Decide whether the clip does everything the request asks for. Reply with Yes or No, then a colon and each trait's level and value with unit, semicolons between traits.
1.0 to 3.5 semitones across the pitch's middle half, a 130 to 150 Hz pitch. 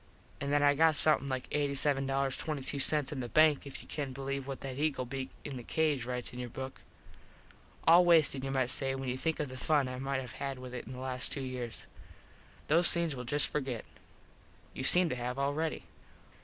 Yes: narrow, 2.4 semitones; low, 135 Hz